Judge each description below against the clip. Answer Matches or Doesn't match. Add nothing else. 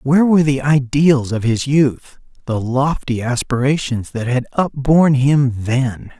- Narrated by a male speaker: Matches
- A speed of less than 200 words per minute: Matches